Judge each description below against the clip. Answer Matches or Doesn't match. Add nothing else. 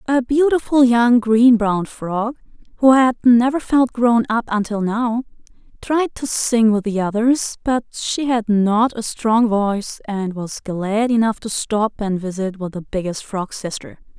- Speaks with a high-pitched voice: Matches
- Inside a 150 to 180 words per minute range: Matches